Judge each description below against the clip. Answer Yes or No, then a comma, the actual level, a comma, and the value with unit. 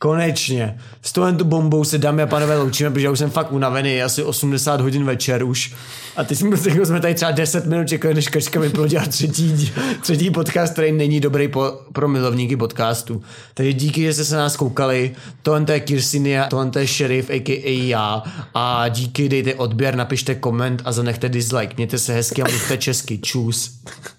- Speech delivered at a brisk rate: Yes, fast, 185 wpm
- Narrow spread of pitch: No, average, 3.3 semitones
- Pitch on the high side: No, low, 135 Hz